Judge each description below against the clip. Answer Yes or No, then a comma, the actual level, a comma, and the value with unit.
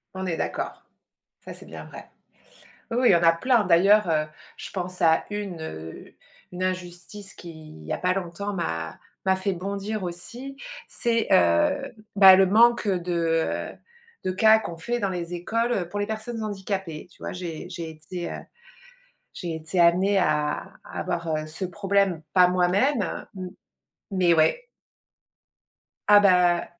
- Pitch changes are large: No, average, 3.2 semitones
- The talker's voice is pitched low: No, medium, 185 Hz